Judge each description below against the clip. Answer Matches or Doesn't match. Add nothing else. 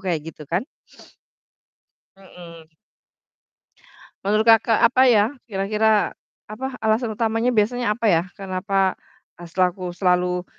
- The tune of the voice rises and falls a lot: Doesn't match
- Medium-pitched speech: Doesn't match